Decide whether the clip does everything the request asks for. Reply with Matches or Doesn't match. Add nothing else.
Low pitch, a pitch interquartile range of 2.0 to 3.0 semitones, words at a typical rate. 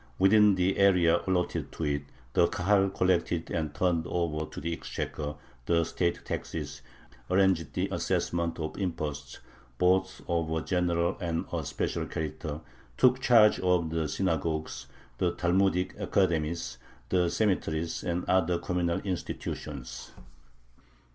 Doesn't match